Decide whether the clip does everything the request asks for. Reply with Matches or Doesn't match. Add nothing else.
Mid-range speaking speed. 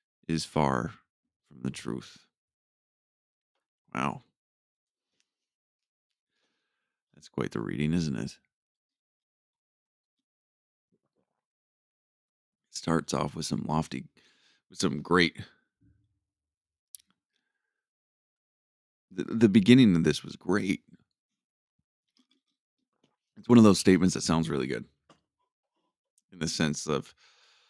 Doesn't match